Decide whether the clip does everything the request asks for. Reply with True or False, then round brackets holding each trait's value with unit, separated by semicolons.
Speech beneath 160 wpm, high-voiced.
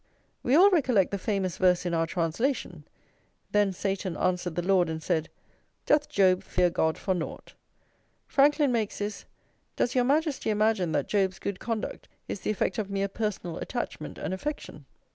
False (165 wpm; 195 Hz)